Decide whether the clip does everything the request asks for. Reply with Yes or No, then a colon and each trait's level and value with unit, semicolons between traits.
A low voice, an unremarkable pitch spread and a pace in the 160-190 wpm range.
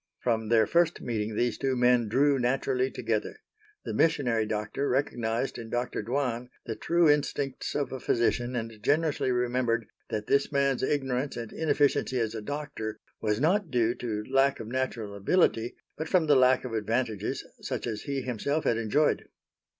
Yes: low, 125 Hz; average, 3.6 semitones; average, 165 wpm